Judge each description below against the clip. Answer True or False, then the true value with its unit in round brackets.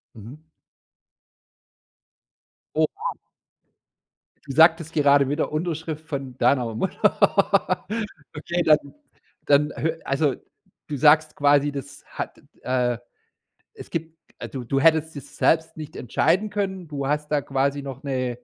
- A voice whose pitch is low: False (150 Hz)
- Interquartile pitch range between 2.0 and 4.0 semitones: True (2.7 semitones)